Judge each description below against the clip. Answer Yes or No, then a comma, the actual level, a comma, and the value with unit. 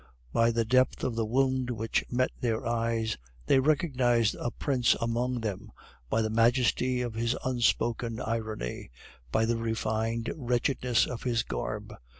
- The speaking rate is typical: Yes, average, 150 wpm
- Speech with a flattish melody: Yes, narrow, 1.9 semitones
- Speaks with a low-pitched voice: Yes, low, 115 Hz